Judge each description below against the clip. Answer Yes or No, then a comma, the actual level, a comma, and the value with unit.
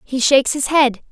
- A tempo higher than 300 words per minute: No, fast, 215 wpm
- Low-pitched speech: No, very high, 265 Hz